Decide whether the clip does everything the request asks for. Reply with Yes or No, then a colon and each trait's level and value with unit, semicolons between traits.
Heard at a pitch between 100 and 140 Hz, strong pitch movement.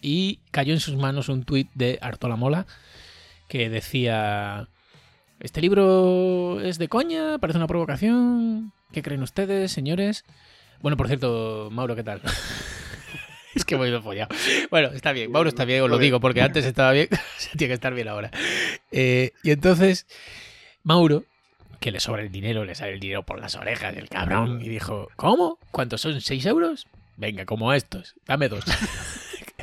Yes: low, 135 Hz; wide, 6.8 semitones